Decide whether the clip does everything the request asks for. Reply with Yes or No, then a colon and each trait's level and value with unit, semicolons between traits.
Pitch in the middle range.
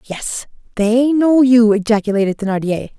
No: high, 225 Hz